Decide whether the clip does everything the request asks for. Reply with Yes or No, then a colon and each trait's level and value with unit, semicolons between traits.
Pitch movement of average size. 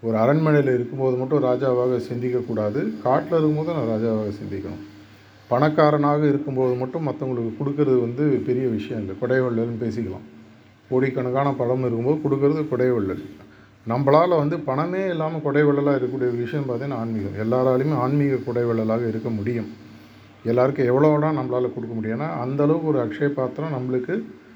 Yes: average, 4.2 semitones